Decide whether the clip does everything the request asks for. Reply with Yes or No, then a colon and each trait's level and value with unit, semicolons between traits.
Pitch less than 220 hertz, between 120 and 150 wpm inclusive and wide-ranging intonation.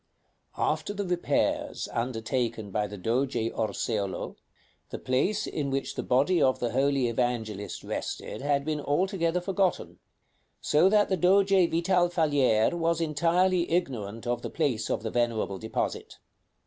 Yes: medium, 140 Hz; average, 140 wpm; wide, 7.1 semitones